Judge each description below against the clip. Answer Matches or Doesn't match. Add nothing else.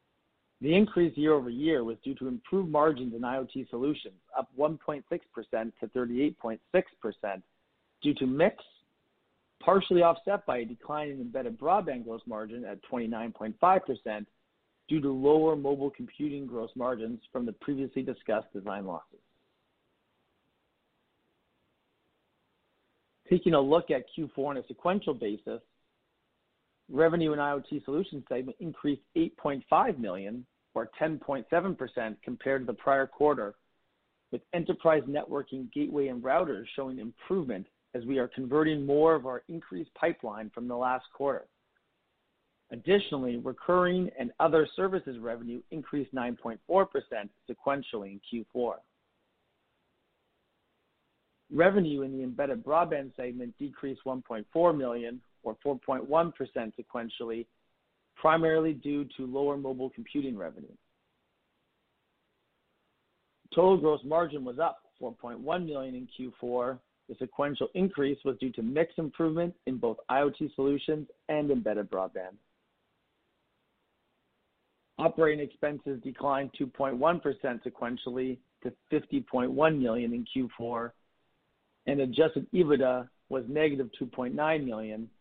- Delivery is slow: Matches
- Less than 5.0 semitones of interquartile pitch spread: Matches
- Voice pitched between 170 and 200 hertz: Doesn't match